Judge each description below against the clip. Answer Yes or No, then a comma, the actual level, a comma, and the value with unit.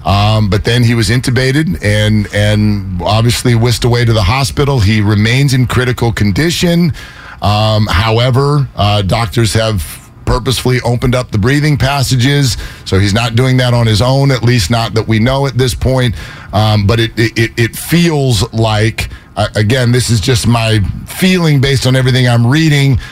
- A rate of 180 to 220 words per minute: No, average, 170 wpm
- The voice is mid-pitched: No, low, 120 Hz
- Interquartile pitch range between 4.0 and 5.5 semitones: No, average, 3.5 semitones